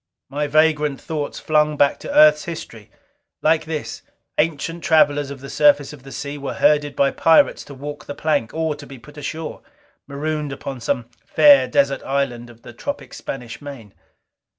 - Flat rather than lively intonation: Yes, narrow, 1.9 semitones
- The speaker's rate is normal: Yes, average, 170 wpm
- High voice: No, medium, 145 Hz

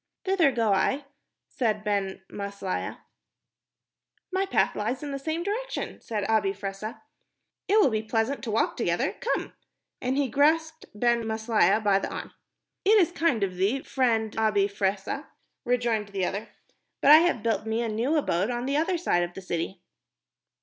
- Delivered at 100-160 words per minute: No, average, 170 wpm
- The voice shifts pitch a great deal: Yes, wide, 5.8 semitones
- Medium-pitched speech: No, high, 225 Hz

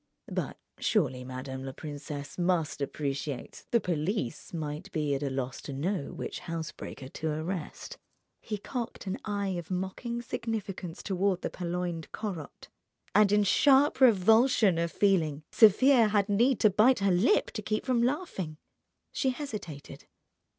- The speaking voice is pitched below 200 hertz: Yes, medium, 185 Hz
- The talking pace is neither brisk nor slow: Yes, average, 145 wpm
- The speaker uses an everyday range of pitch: No, wide, 5.9 semitones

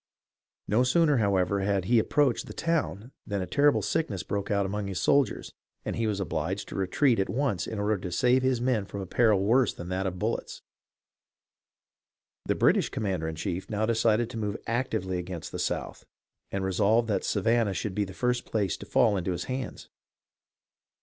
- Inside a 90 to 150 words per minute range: No, average, 190 wpm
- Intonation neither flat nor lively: Yes, average, 3.9 semitones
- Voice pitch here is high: No, low, 105 Hz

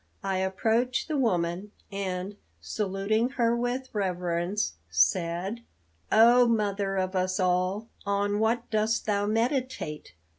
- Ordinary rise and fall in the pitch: Yes, average, 3.6 semitones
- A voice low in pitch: No, high, 200 Hz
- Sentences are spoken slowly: Yes, slow, 115 wpm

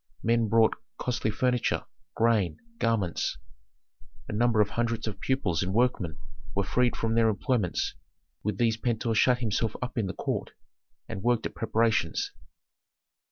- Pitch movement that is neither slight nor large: No, narrow, 2.3 semitones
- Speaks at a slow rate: No, average, 145 wpm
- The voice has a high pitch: No, low, 115 Hz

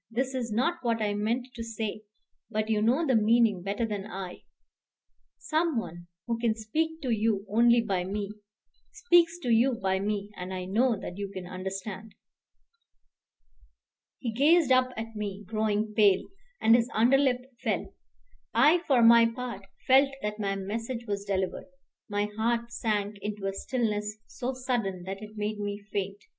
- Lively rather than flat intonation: No, average, 3.0 semitones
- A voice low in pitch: No, high, 220 Hz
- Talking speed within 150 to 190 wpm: Yes, average, 160 wpm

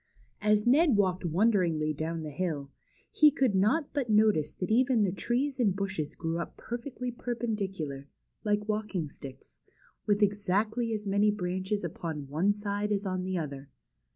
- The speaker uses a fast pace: No, average, 165 wpm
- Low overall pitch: No, high, 200 Hz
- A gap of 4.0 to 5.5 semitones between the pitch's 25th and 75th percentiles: Yes, average, 4.3 semitones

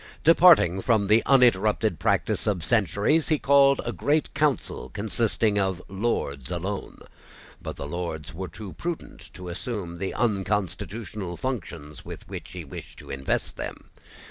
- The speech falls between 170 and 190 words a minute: No, average, 145 wpm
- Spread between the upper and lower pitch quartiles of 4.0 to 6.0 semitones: Yes, wide, 5.5 semitones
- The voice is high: No, low, 100 Hz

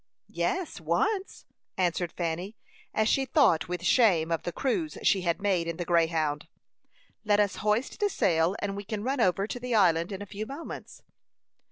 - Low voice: No, high, 195 Hz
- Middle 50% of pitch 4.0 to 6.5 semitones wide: Yes, wide, 5.4 semitones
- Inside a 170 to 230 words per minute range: Yes, average, 180 wpm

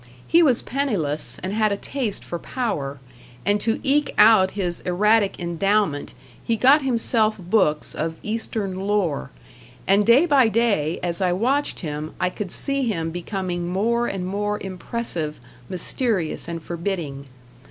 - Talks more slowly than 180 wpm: Yes, average, 145 wpm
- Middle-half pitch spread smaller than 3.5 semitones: No, average, 4.9 semitones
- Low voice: No, high, 200 Hz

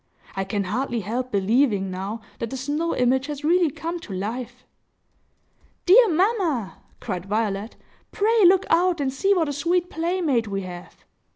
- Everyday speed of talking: Yes, average, 160 wpm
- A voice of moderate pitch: No, very high, 265 Hz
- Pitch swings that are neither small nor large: No, wide, 8.4 semitones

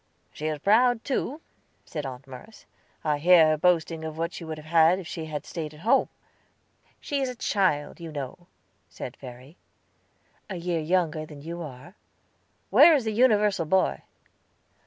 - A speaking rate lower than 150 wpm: No, average, 170 wpm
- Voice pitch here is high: No, medium, 165 Hz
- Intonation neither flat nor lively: Yes, average, 3.9 semitones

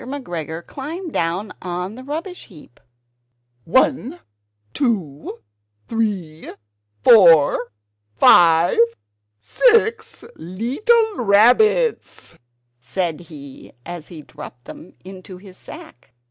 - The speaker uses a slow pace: Yes, slow, 90 wpm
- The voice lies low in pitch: No, high, 190 Hz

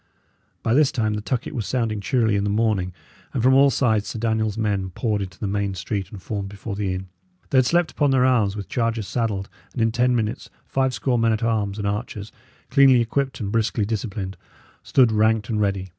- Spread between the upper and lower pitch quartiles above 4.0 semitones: No, average, 3.1 semitones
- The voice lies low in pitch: Yes, low, 110 Hz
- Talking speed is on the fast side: Yes, fast, 215 wpm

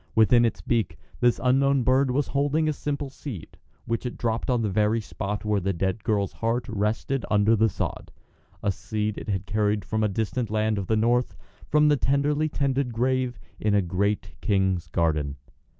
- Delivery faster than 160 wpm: Yes, average, 185 wpm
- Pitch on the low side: Yes, low, 110 Hz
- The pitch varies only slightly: No, average, 4.0 semitones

